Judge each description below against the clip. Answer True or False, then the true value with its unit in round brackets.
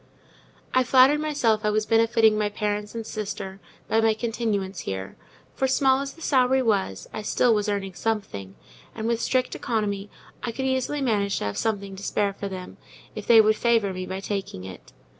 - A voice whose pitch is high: True (215 Hz)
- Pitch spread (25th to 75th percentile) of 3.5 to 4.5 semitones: False (3.1 semitones)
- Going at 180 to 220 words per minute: True (190 wpm)